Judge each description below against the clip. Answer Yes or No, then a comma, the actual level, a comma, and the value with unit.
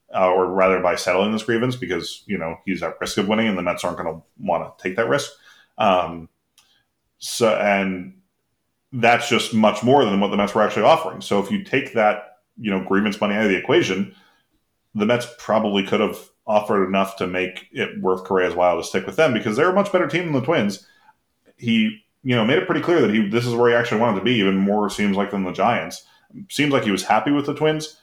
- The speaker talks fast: Yes, fast, 240 wpm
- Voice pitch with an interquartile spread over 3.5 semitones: Yes, average, 4.7 semitones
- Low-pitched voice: Yes, low, 105 Hz